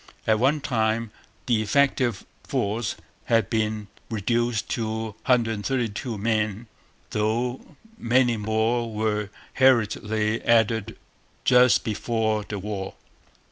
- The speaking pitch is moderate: No, low, 110 Hz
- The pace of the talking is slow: Yes, slow, 100 wpm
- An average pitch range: No, narrow, 1.9 semitones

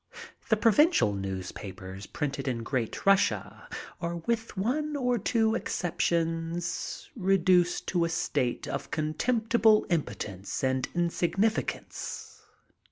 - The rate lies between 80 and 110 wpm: Yes, slow, 105 wpm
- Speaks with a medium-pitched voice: Yes, medium, 170 Hz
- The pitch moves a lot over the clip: Yes, wide, 8.7 semitones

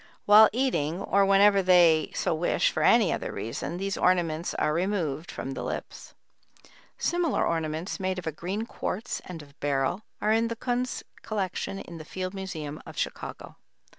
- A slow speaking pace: No, average, 165 wpm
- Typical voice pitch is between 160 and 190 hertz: Yes, medium, 185 Hz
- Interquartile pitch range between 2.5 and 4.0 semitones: No, average, 4.4 semitones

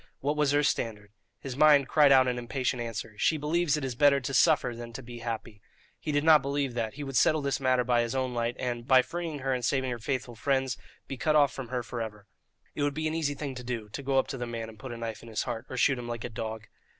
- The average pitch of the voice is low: Yes, low, 130 Hz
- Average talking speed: No, fast, 280 wpm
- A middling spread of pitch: Yes, average, 3.2 semitones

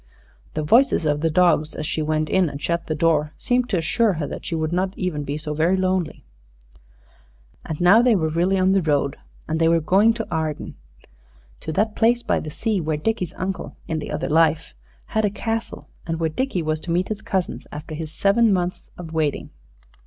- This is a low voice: No, medium, 165 Hz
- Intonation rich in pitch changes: No, average, 3.7 semitones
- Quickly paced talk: Yes, fast, 210 wpm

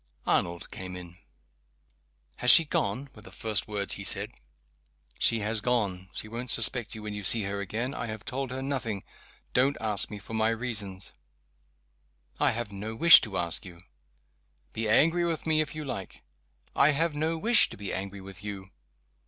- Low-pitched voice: Yes, low, 110 Hz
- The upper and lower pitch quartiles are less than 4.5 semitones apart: No, average, 4.8 semitones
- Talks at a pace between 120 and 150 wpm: No, average, 180 wpm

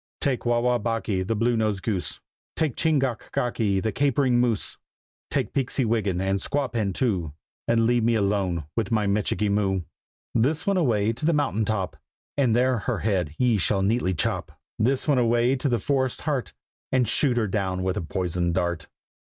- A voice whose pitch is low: Yes, low, 115 Hz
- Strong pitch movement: No, average, 4.3 semitones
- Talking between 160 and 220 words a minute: Yes, average, 185 wpm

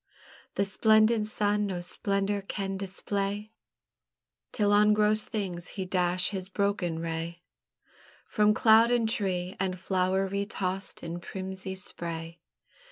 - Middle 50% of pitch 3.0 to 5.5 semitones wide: No, narrow, 2.4 semitones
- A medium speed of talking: No, slow, 125 wpm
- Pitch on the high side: Yes, high, 195 Hz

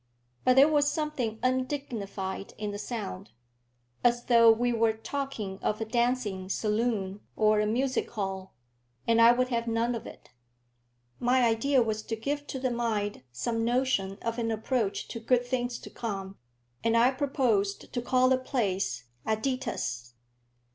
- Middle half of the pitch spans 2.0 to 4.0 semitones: Yes, average, 3.2 semitones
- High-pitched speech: Yes, high, 230 Hz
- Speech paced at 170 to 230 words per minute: No, average, 155 wpm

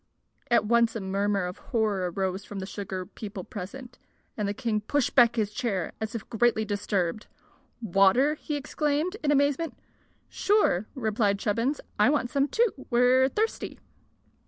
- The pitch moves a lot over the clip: No, average, 4.9 semitones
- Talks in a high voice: Yes, high, 225 Hz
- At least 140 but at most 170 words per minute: Yes, average, 155 wpm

